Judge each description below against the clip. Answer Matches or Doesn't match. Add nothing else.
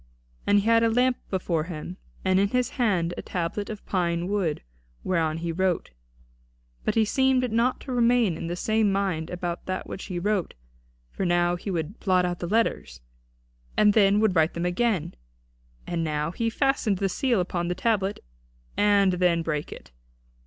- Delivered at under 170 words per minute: Doesn't match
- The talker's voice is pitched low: Doesn't match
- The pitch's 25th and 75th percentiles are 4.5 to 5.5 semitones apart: Doesn't match